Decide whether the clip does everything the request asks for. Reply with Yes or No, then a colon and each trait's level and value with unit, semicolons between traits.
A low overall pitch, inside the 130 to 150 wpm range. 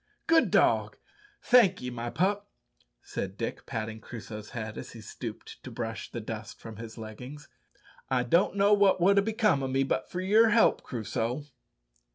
No: low, 130 Hz; average, 170 wpm